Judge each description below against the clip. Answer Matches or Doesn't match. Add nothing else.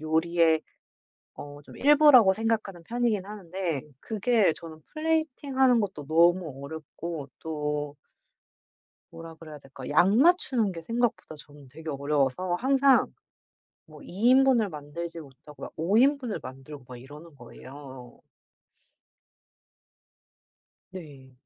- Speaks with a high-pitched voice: Doesn't match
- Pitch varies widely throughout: Matches